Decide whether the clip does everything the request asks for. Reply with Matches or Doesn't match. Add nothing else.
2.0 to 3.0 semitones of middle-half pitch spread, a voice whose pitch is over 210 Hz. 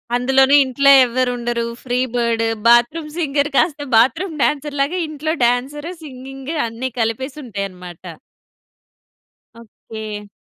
Doesn't match